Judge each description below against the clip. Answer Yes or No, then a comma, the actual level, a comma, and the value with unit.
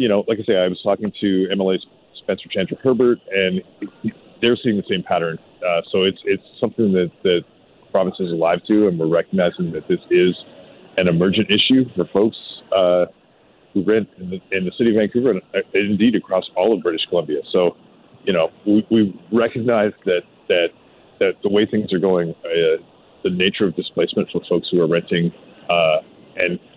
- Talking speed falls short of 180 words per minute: No, average, 190 wpm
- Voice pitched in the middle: No, low, 100 Hz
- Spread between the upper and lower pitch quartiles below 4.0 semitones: No, average, 4.6 semitones